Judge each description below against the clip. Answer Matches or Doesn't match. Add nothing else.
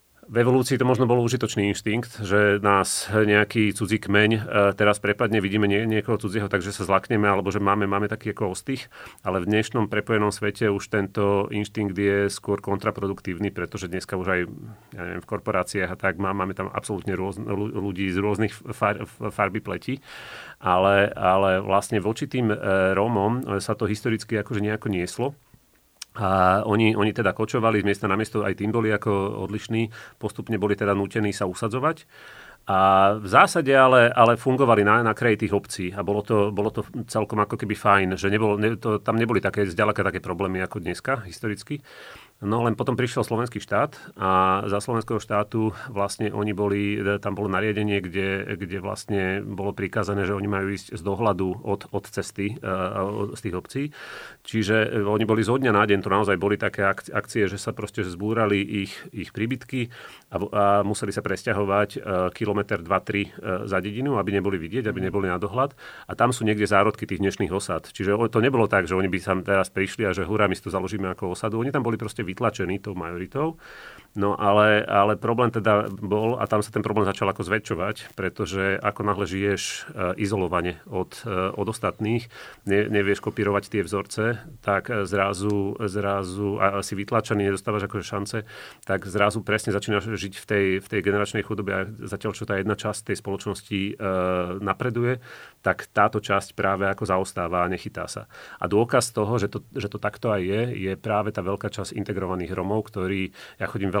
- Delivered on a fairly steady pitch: Matches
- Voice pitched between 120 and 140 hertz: Doesn't match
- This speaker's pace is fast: Matches